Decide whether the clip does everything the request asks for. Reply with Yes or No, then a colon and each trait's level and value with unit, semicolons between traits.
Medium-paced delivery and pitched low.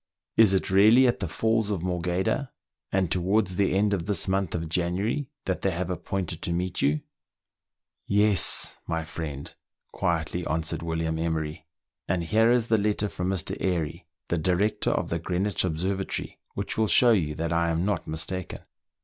Yes: average, 175 wpm; very low, 90 Hz